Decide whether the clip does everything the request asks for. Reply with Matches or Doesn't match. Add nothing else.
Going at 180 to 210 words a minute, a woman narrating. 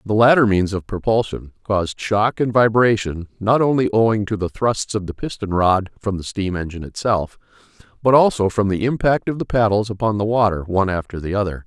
Doesn't match